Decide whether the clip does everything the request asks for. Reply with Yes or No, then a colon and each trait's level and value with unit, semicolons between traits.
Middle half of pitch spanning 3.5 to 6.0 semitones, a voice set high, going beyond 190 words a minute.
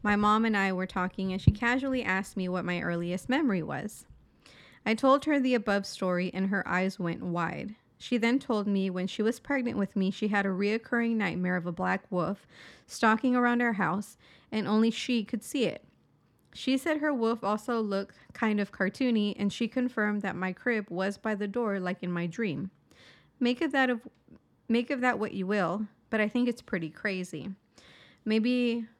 Yes: average, 3.9 semitones; high, 210 Hz; average, 200 wpm